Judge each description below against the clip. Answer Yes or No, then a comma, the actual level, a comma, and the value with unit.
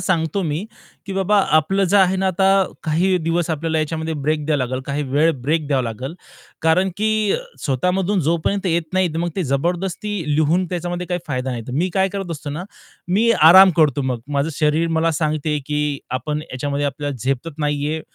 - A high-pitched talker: No, medium, 160 Hz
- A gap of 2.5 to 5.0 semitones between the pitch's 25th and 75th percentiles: Yes, average, 3.8 semitones